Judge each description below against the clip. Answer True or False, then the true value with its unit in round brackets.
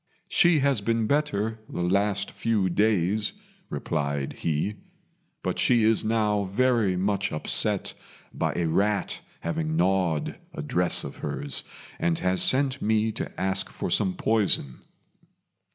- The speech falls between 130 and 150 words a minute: True (135 wpm)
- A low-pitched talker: True (100 Hz)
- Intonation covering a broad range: False (4.1 semitones)